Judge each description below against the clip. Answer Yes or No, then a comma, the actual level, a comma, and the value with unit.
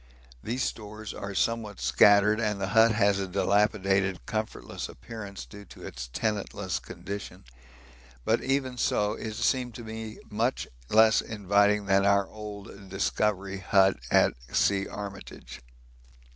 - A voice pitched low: Yes, low, 105 Hz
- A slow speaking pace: Yes, slow, 130 wpm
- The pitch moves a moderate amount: No, narrow, 1.8 semitones